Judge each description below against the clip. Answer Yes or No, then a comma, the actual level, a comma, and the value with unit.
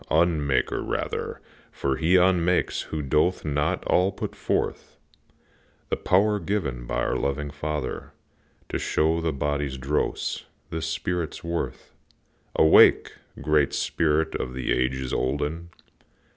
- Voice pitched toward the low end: Yes, very low, 75 Hz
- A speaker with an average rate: No, slow, 120 wpm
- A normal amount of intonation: Yes, average, 3.3 semitones